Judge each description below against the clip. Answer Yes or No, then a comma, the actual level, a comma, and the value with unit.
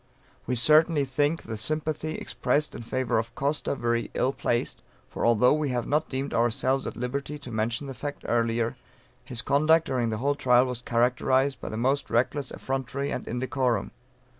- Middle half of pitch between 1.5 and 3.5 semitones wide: Yes, average, 3.2 semitones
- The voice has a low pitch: Yes, low, 130 Hz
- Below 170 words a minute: No, average, 175 wpm